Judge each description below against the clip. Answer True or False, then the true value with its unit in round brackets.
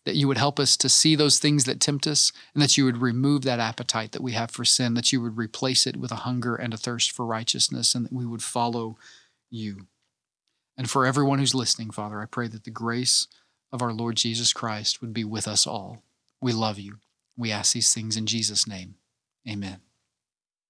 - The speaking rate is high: True (215 wpm)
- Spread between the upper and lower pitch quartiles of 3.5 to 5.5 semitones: False (2.6 semitones)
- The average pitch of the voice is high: False (120 Hz)